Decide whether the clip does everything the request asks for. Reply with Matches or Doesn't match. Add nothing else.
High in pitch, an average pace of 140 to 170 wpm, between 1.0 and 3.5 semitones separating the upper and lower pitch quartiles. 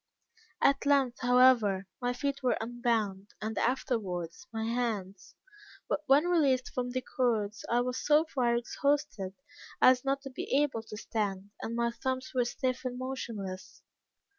Matches